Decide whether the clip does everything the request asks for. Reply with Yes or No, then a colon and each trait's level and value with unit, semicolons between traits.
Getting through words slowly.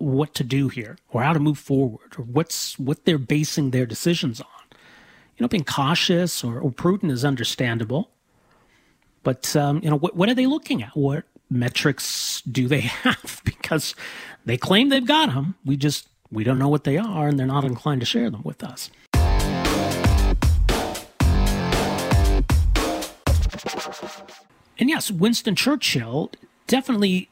No: average, 150 wpm